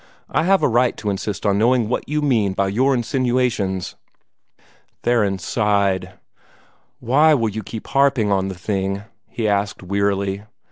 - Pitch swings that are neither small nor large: Yes, average, 4.1 semitones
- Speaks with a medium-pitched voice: No, low, 105 Hz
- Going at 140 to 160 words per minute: Yes, average, 150 wpm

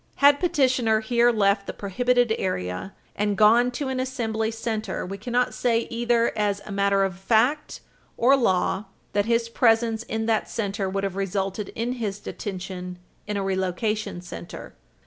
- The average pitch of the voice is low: No, high, 220 Hz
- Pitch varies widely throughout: No, average, 3.4 semitones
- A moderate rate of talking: Yes, average, 160 wpm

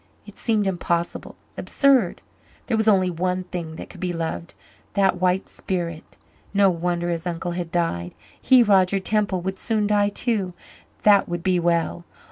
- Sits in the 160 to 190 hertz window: Yes, medium, 185 Hz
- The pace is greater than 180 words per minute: No, average, 160 wpm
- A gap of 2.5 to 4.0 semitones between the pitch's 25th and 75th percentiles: Yes, average, 2.8 semitones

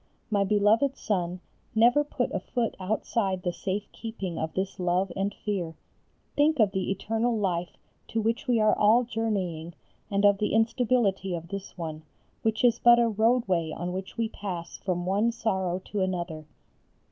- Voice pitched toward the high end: Yes, high, 200 Hz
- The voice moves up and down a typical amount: Yes, average, 3.8 semitones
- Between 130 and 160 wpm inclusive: No, average, 170 wpm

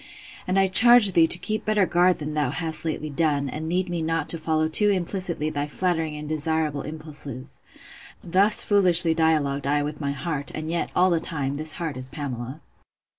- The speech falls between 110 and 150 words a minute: No, average, 190 wpm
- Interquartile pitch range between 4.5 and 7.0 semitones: No, average, 3.1 semitones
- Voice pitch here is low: No, medium, 160 Hz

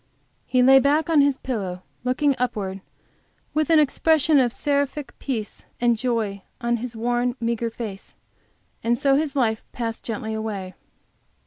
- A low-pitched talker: No, high, 245 Hz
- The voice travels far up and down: No, average, 3.9 semitones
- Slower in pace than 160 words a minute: Yes, average, 145 wpm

